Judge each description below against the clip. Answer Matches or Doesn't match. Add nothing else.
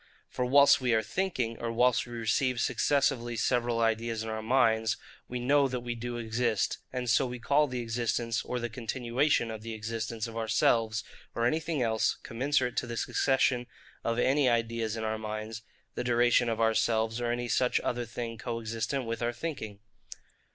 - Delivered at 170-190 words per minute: Matches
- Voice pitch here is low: Matches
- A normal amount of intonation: Doesn't match